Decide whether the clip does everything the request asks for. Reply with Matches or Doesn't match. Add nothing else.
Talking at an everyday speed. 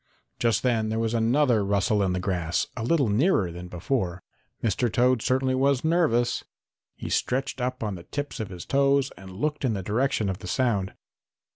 Matches